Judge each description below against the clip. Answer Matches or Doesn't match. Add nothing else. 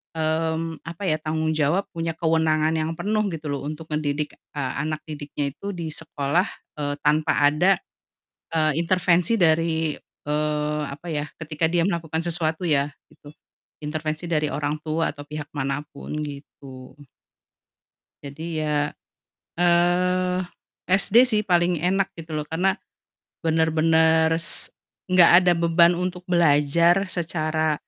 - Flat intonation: Matches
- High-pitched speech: Doesn't match